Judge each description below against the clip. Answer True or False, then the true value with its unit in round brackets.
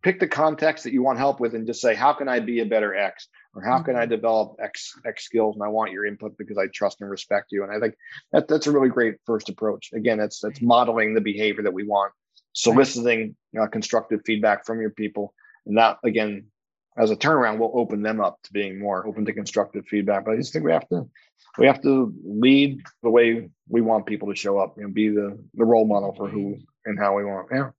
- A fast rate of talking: True (245 wpm)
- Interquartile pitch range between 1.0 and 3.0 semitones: True (2.5 semitones)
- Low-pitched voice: True (110 Hz)